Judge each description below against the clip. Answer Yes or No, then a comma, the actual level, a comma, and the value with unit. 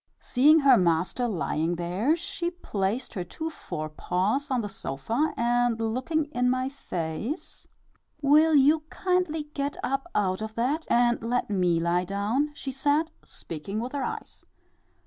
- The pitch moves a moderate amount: No, wide, 7.2 semitones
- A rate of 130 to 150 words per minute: Yes, average, 145 wpm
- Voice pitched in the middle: No, high, 245 Hz